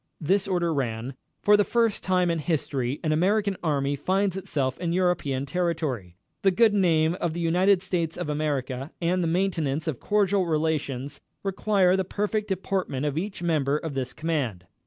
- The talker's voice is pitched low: No, medium, 165 Hz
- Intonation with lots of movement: No, average, 5.0 semitones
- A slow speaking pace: No, average, 170 wpm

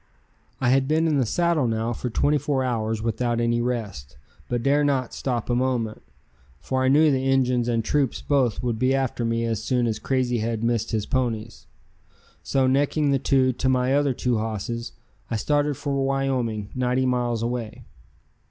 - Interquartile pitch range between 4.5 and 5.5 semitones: No, narrow, 2.6 semitones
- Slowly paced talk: No, average, 180 wpm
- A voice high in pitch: No, low, 125 Hz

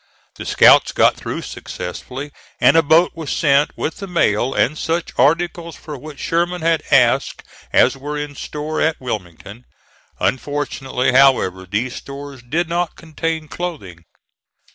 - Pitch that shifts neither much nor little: Yes, average, 4.3 semitones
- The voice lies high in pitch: No, medium, 145 Hz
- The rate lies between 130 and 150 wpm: Yes, average, 140 wpm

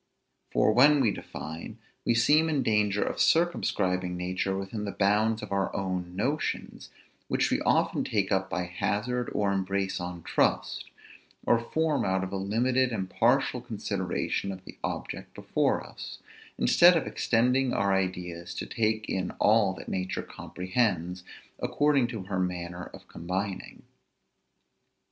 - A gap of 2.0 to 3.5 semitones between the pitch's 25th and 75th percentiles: No, average, 4.2 semitones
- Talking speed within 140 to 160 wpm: Yes, average, 145 wpm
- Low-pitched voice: Yes, low, 100 Hz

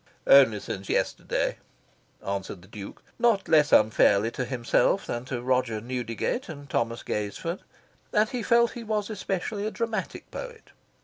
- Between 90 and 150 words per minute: Yes, average, 145 wpm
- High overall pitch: No, low, 135 Hz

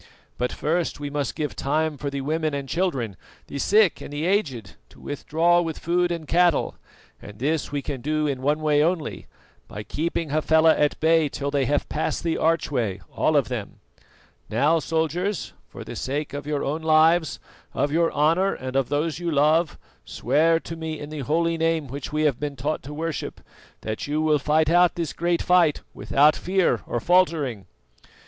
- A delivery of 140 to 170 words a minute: No, average, 185 wpm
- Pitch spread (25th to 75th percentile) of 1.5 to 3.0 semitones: Yes, narrow, 2.5 semitones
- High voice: No, medium, 155 Hz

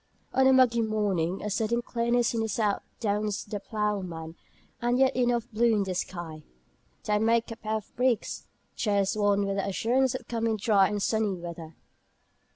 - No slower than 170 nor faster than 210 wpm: Yes, average, 175 wpm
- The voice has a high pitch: Yes, high, 215 Hz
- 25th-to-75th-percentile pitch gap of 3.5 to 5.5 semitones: No, average, 3.0 semitones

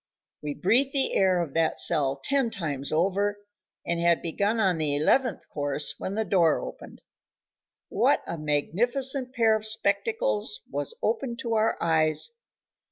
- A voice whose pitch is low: No, high, 195 Hz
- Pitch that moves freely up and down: Yes, wide, 7.2 semitones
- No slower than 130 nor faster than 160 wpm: Yes, average, 150 wpm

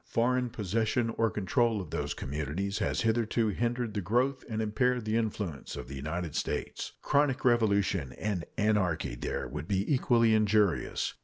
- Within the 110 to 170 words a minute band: Yes, average, 155 wpm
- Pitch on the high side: No, low, 110 Hz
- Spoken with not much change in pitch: No, average, 3.7 semitones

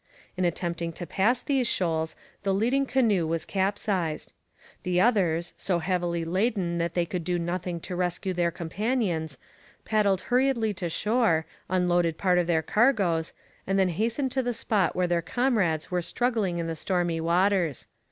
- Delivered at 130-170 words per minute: Yes, average, 160 wpm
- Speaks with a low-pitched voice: No, medium, 180 Hz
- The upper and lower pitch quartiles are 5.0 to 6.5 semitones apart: No, average, 3.8 semitones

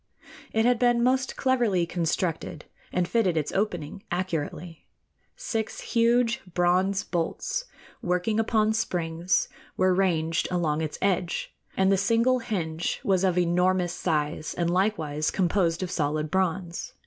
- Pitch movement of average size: Yes, average, 4.5 semitones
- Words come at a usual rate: No, slow, 130 wpm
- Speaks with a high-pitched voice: No, medium, 180 Hz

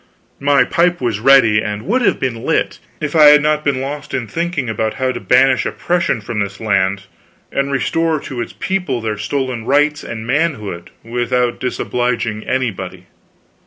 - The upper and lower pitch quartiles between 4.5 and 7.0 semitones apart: Yes, average, 4.9 semitones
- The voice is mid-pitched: No, low, 125 Hz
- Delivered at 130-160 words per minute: No, average, 170 wpm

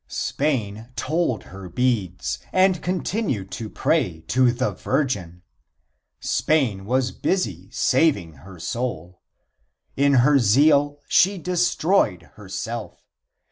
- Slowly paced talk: Yes, slow, 100 wpm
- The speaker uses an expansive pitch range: Yes, wide, 7.5 semitones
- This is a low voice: Yes, low, 120 Hz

